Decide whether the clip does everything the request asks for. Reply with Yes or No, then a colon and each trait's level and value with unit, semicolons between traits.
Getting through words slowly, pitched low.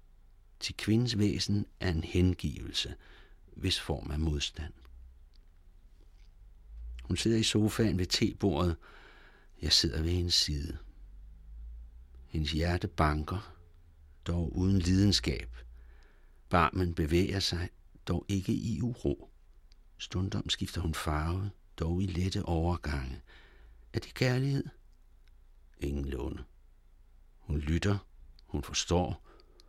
Yes: slow, 105 wpm; very low, 85 Hz